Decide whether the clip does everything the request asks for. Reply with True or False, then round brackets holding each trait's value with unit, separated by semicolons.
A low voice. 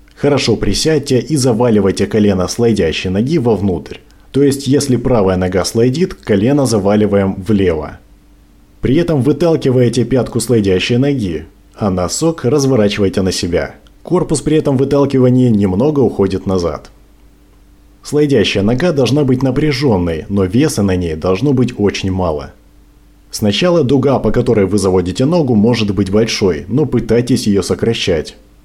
True (115 Hz)